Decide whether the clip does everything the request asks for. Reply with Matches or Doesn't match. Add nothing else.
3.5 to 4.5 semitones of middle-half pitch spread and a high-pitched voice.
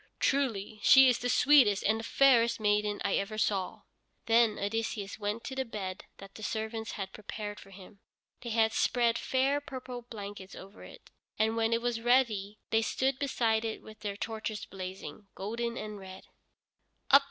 Doesn't match